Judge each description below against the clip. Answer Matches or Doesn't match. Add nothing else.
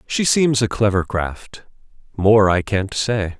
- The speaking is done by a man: Matches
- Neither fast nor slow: Matches